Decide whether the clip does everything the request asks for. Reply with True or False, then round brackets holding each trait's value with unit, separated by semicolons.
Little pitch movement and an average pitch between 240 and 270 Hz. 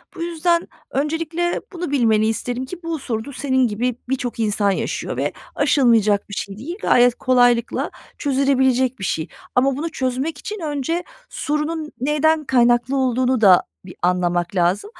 False (4.9 semitones; 260 Hz)